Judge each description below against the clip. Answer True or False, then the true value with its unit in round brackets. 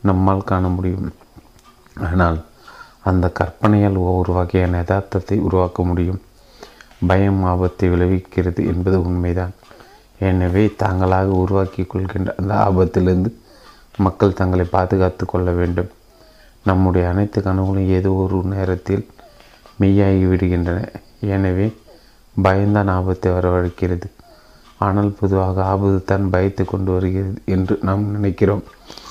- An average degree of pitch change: False (1.3 semitones)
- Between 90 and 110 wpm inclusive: True (100 wpm)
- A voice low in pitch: True (95 Hz)